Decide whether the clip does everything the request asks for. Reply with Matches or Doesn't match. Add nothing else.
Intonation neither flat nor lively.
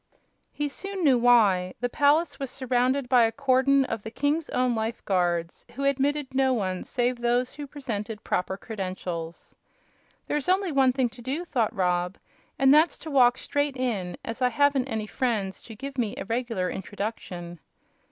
Matches